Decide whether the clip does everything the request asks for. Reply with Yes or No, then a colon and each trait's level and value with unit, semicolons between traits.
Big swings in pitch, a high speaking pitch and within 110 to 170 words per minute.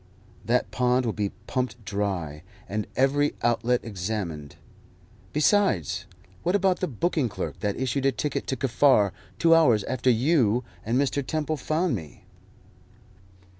No: wide, 5.7 semitones; low, 125 Hz; slow, 135 wpm